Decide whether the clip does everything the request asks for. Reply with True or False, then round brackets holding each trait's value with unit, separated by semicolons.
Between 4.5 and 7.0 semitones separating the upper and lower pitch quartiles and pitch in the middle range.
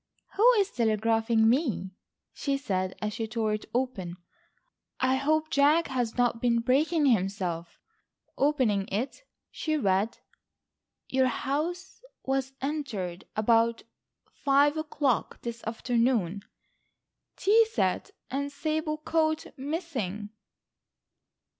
False (5.5 semitones; 255 Hz)